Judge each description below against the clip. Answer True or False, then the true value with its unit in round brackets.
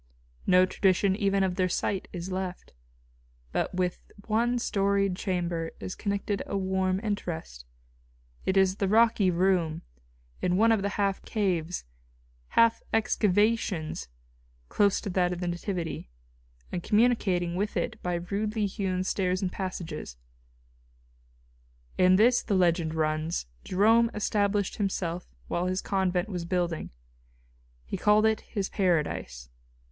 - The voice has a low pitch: False (190 Hz)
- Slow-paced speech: True (130 wpm)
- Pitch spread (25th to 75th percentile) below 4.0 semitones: True (2.5 semitones)